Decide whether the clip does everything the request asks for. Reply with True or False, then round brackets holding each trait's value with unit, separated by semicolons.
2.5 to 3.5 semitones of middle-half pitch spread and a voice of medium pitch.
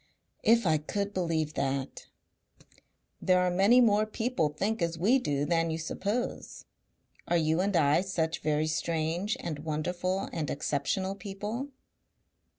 False (4.3 semitones; 175 Hz)